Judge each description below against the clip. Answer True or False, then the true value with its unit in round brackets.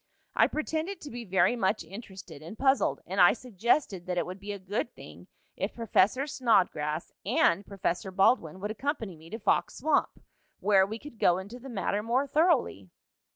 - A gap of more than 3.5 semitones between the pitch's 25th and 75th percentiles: True (5.3 semitones)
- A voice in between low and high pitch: False (205 Hz)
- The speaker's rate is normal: True (180 wpm)